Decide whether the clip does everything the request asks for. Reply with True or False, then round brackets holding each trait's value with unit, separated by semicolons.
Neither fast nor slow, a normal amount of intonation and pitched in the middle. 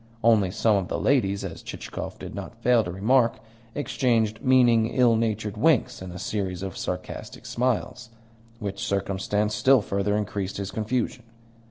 False (155 wpm; 3.5 semitones; 105 Hz)